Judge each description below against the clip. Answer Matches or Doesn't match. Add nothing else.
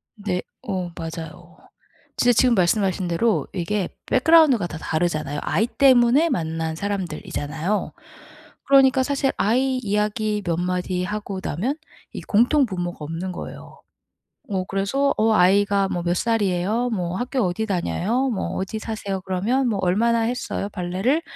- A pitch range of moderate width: Matches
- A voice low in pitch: Doesn't match